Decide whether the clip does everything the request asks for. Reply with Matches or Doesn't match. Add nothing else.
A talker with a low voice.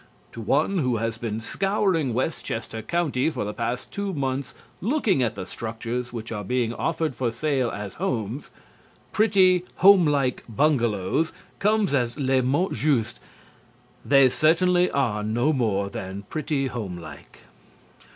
Matches